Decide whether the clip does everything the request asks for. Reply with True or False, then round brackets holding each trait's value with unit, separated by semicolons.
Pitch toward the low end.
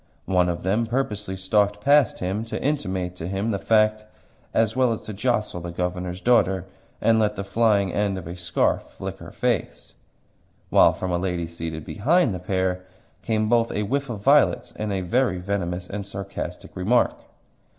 True (100 Hz)